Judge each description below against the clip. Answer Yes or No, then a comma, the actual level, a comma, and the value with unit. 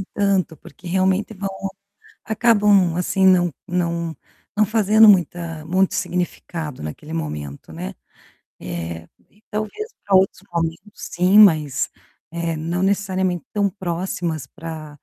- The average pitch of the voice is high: No, medium, 180 Hz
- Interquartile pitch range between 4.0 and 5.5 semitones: No, average, 3.3 semitones